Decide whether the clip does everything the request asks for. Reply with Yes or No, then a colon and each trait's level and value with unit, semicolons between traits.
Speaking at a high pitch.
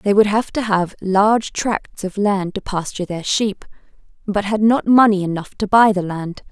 Yes: high, 200 Hz